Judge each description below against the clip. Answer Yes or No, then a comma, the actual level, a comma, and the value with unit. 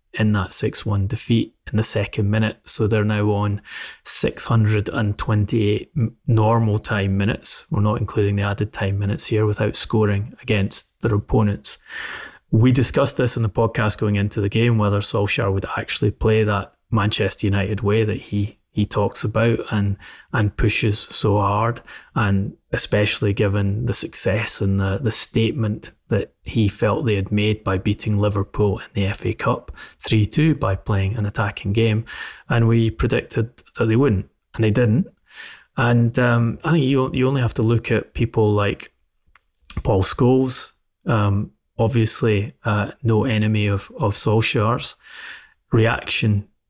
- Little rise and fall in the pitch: Yes, narrow, 2.0 semitones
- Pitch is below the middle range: Yes, low, 110 Hz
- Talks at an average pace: Yes, average, 155 wpm